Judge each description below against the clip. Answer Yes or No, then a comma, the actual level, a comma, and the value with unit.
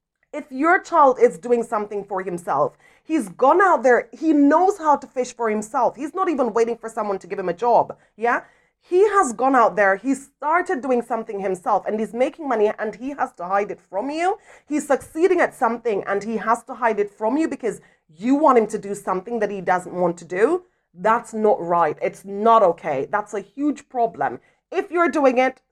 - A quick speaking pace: Yes, fast, 215 wpm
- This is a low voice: No, high, 240 Hz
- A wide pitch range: Yes, wide, 5.9 semitones